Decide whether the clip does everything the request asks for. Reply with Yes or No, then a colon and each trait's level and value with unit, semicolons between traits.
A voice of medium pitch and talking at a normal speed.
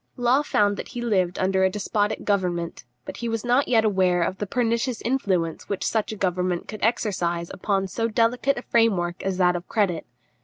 No: high, 200 Hz; average, 195 wpm